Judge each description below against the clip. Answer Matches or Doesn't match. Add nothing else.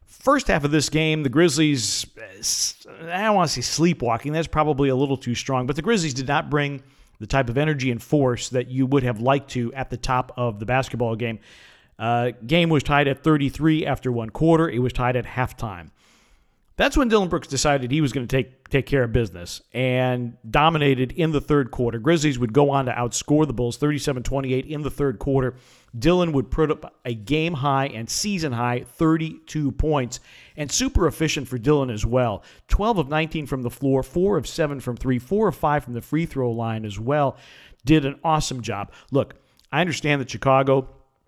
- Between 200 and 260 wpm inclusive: Matches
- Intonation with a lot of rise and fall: Doesn't match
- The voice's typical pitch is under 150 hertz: Matches